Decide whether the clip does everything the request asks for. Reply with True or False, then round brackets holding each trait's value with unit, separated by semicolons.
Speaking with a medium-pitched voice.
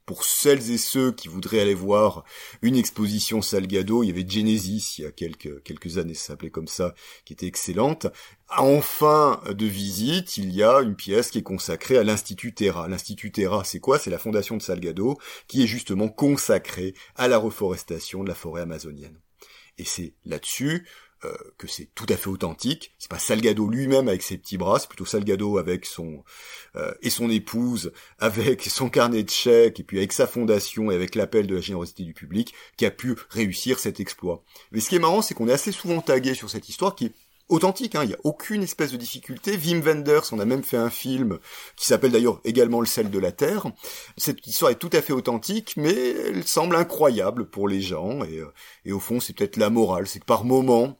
False (110 Hz)